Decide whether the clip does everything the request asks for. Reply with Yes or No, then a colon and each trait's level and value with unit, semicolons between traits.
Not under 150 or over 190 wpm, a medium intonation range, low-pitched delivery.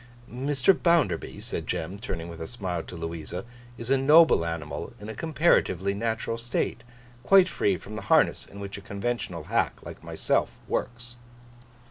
No: average, 160 wpm; wide, 5.8 semitones; low, 105 Hz